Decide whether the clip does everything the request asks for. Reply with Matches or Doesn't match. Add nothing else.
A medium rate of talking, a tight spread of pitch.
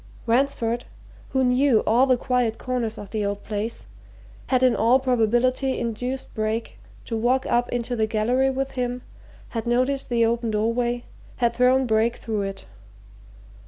Matches